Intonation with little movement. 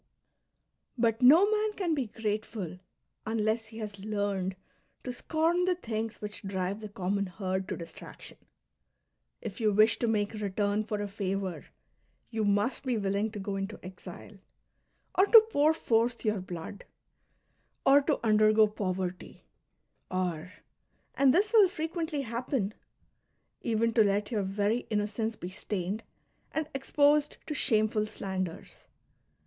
No: average, 3.8 semitones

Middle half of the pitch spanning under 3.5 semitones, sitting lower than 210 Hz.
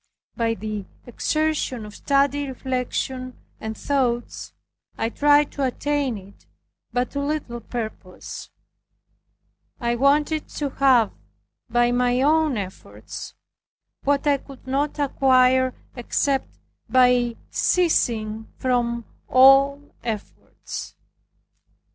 No: average, 3.0 semitones; very high, 255 Hz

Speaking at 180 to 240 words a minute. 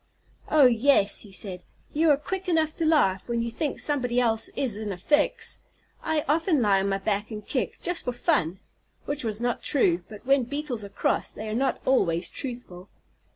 Yes: average, 200 wpm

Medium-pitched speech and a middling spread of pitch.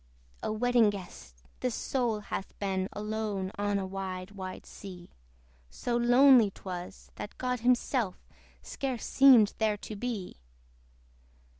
No: high, 210 Hz; average, 4.2 semitones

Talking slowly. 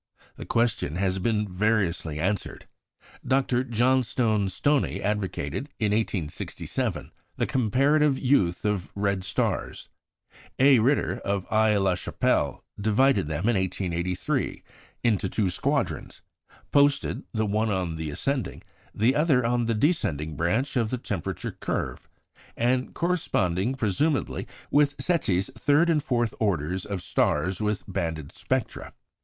Yes: slow, 125 wpm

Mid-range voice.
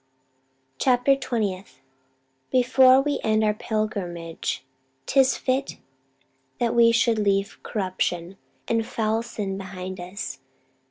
No: high, 215 Hz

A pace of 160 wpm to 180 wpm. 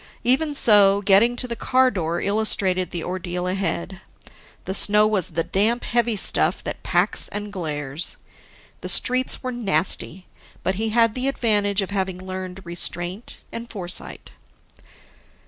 No: average, 145 wpm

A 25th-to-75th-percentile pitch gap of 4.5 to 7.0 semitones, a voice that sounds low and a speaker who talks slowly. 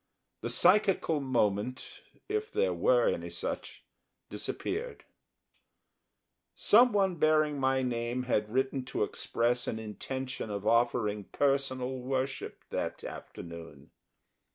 Yes: average, 5.0 semitones; low, 130 Hz; slow, 105 wpm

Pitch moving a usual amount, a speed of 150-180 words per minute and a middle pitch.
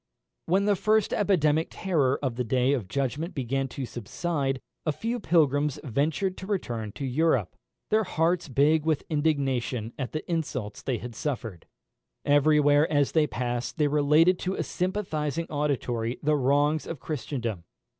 Yes: average, 4.1 semitones; average, 155 wpm; medium, 145 Hz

